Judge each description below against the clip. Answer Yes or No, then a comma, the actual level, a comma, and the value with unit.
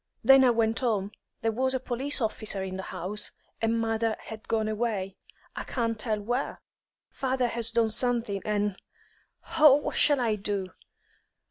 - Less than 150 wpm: No, average, 160 wpm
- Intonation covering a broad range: No, average, 2.7 semitones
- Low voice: No, high, 225 Hz